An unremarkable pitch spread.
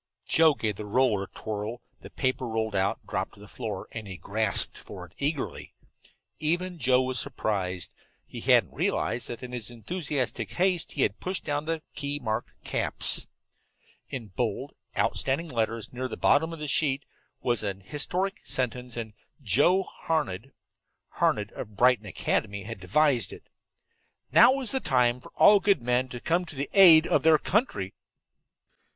No: wide, 6.1 semitones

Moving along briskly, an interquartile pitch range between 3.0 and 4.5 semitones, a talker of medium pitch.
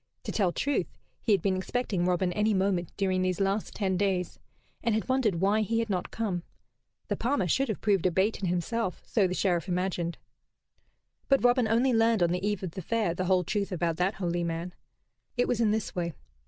No: fast, 210 wpm; average, 3.6 semitones; high, 195 Hz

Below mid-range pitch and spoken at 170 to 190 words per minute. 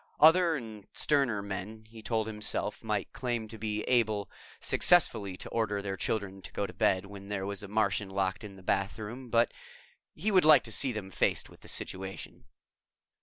Yes: low, 105 Hz; average, 185 wpm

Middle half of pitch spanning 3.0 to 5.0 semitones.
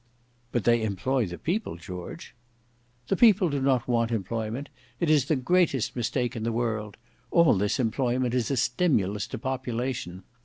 Yes: average, 3.7 semitones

